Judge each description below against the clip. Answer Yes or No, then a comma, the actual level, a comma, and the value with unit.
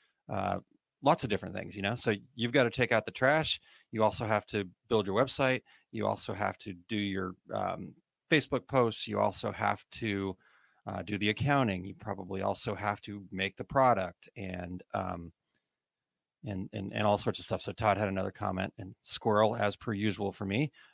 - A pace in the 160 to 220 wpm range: Yes, average, 195 wpm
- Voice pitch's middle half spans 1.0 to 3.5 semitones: Yes, average, 3.1 semitones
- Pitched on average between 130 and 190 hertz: No, low, 105 Hz